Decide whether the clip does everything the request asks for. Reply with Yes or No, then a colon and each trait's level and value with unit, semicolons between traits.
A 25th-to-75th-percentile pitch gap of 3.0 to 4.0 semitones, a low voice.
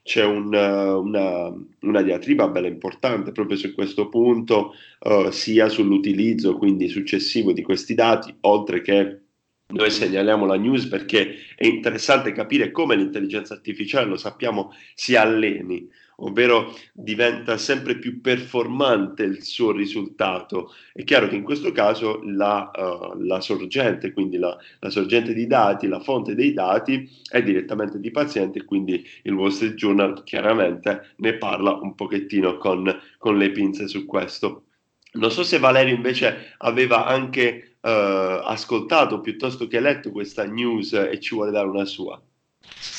No: average, 4.4 semitones; low, 110 Hz